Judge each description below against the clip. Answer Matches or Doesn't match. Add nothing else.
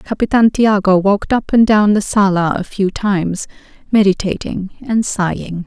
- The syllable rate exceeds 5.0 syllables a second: Doesn't match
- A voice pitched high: Matches